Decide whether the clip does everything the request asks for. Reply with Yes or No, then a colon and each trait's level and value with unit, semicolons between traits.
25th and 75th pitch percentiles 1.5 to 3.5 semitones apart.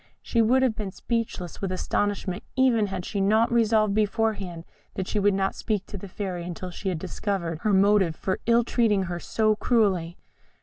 Yes: average, 3.0 semitones